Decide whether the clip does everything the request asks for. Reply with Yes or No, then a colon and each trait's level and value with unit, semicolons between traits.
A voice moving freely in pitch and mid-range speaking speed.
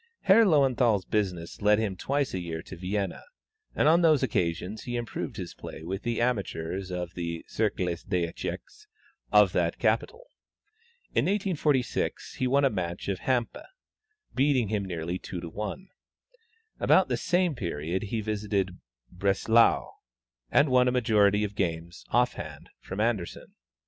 Yes: wide, 5.8 semitones; average, 150 wpm